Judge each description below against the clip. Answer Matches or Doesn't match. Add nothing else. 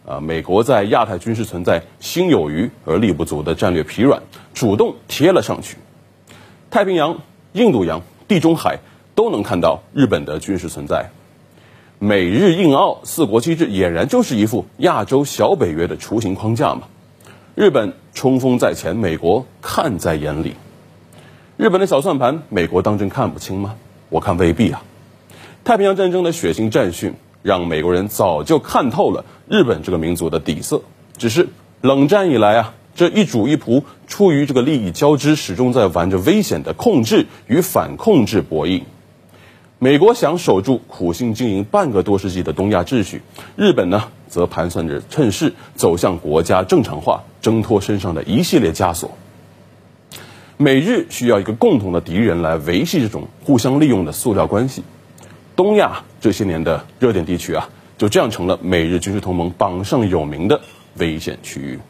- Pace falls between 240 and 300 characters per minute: Matches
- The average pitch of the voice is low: Matches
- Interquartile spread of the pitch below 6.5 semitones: Doesn't match